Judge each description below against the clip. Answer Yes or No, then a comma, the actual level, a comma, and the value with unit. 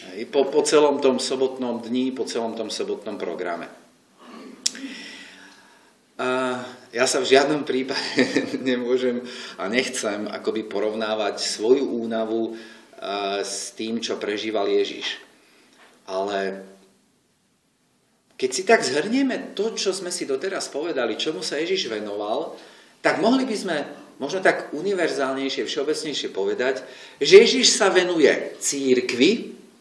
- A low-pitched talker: No, medium, 150 Hz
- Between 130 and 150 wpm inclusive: No, average, 115 wpm